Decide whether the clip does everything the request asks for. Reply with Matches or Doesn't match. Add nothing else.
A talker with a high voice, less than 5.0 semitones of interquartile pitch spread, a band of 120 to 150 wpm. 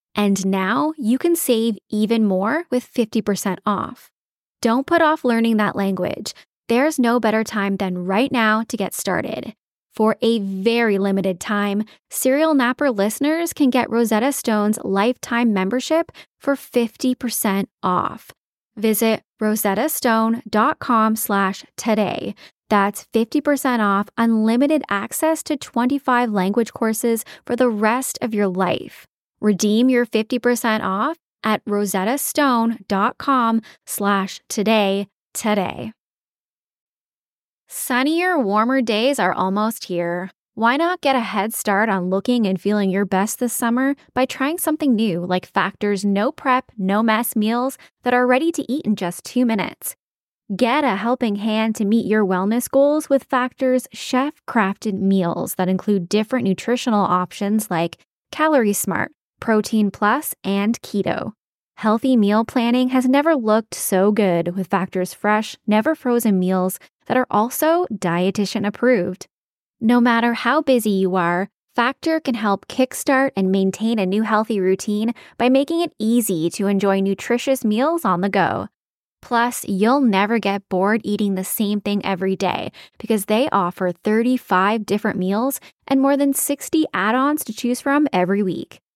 Matches